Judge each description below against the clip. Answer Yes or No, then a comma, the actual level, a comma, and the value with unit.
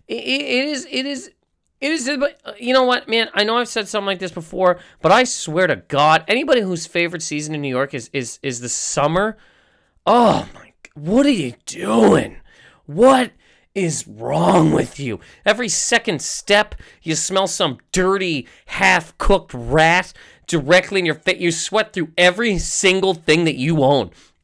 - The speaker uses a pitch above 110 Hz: Yes, medium, 185 Hz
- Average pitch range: No, wide, 5.8 semitones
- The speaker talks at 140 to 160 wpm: No, average, 170 wpm